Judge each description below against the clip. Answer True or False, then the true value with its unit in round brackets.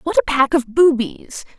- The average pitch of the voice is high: True (275 Hz)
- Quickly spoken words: False (190 wpm)